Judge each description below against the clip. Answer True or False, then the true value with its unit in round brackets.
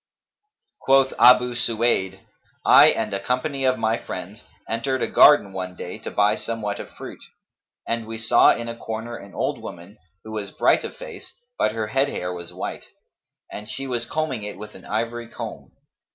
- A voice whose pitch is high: False (115 Hz)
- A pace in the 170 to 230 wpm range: True (180 wpm)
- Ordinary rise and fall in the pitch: True (3.1 semitones)